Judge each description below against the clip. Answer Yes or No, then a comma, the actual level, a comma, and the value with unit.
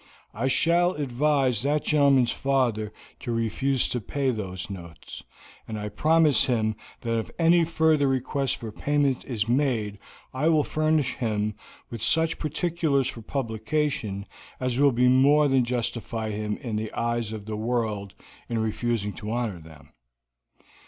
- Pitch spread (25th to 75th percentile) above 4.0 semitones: Yes, average, 4.7 semitones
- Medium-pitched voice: No, low, 125 Hz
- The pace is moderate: Yes, average, 145 wpm